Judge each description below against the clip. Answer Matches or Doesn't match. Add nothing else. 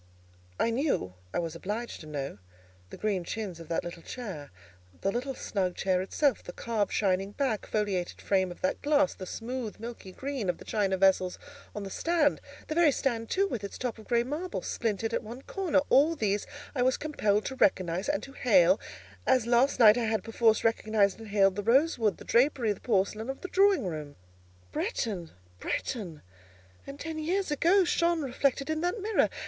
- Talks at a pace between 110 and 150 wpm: Doesn't match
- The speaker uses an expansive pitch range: Matches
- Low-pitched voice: Doesn't match